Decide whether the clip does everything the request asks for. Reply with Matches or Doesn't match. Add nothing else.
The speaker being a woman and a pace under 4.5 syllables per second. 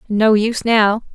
Matches